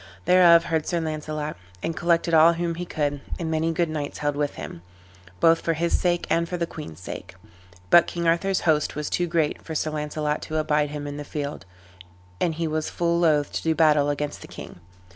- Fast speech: Yes, fast, 210 wpm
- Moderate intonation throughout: No, narrow, 2.2 semitones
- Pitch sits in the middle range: Yes, medium, 155 Hz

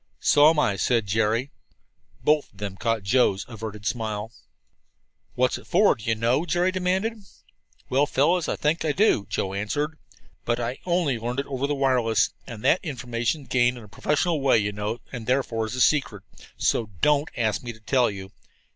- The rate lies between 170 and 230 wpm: Yes, average, 180 wpm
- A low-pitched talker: Yes, low, 120 Hz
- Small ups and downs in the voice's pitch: No, average, 4.9 semitones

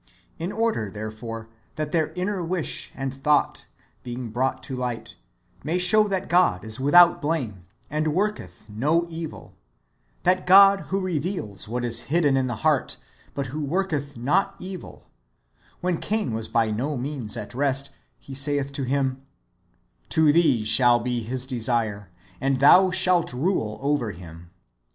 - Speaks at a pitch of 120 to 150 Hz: Yes, medium, 140 Hz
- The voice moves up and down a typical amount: No, wide, 6.5 semitones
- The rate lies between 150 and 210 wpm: Yes, average, 160 wpm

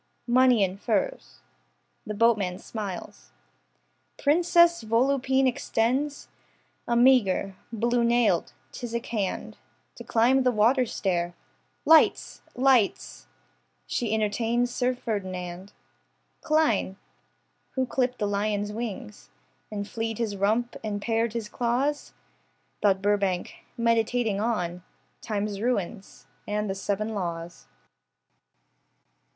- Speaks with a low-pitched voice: No, high, 225 Hz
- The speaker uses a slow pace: Yes, slow, 100 wpm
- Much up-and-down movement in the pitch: No, average, 3.5 semitones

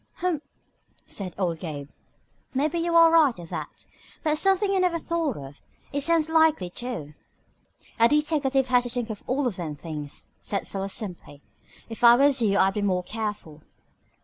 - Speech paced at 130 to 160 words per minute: No, average, 170 wpm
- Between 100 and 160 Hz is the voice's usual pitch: No, high, 240 Hz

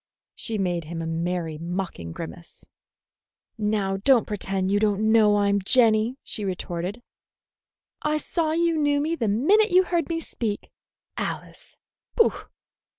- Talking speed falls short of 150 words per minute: Yes, average, 140 wpm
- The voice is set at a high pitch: Yes, high, 210 Hz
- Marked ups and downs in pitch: Yes, wide, 7.5 semitones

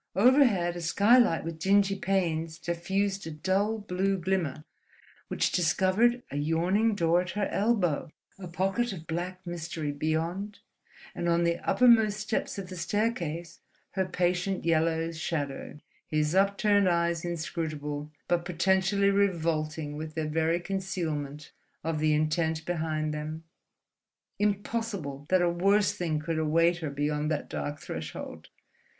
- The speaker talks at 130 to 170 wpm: Yes, slow, 135 wpm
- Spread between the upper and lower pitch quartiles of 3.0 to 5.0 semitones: Yes, average, 3.6 semitones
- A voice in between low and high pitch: Yes, medium, 175 Hz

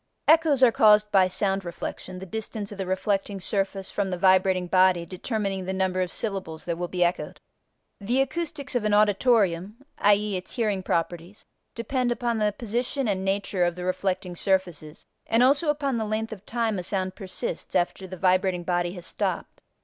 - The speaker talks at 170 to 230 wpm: Yes, average, 180 wpm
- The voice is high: Yes, high, 195 Hz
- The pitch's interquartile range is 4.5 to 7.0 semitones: No, average, 3.2 semitones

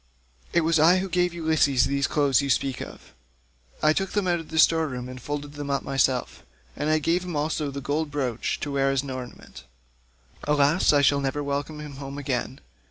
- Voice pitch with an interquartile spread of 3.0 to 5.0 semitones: No, narrow, 2.5 semitones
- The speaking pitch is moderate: Yes, medium, 145 Hz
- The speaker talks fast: Yes, fast, 210 wpm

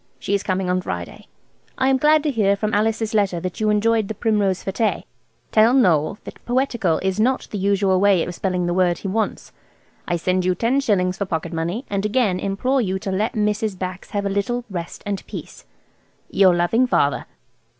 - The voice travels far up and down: No, average, 3.3 semitones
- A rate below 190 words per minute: No, average, 200 wpm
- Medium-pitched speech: No, high, 200 Hz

